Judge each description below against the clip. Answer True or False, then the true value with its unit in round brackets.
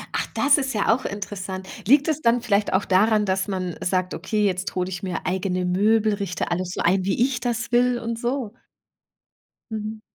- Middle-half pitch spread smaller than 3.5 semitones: False (3.8 semitones)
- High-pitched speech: True (205 Hz)